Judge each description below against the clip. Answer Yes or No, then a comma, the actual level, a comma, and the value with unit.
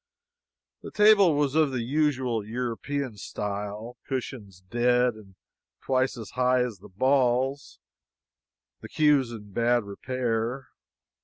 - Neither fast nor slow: No, slow, 120 wpm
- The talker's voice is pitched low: Yes, low, 125 Hz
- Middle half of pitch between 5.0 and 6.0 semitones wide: No, average, 3.3 semitones